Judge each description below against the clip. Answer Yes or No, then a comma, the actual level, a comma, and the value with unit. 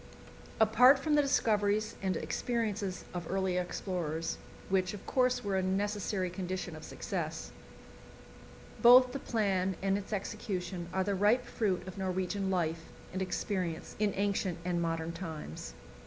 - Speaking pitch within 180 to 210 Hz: Yes, high, 190 Hz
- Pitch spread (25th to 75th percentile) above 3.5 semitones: No, average, 2.7 semitones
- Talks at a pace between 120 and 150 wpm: Yes, average, 140 wpm